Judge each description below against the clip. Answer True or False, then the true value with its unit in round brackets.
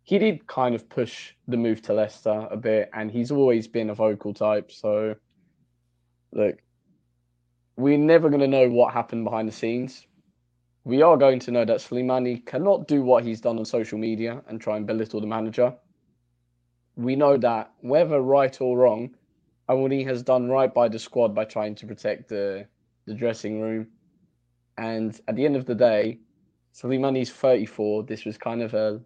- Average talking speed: True (180 wpm)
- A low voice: True (115 Hz)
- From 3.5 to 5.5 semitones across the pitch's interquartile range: False (3.0 semitones)